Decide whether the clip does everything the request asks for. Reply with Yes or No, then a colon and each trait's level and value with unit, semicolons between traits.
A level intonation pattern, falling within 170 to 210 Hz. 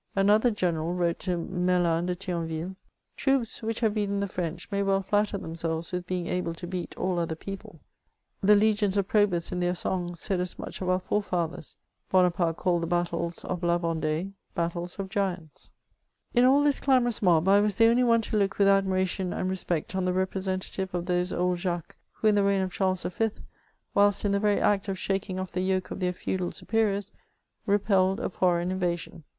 Yes: narrow, 2.3 semitones; medium, 185 Hz